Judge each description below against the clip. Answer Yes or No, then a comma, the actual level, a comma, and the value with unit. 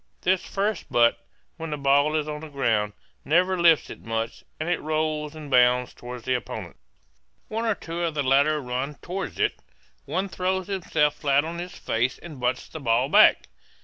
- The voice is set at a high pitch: No, medium, 150 Hz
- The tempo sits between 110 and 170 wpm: No, average, 185 wpm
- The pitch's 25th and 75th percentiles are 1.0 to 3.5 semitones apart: No, average, 5.0 semitones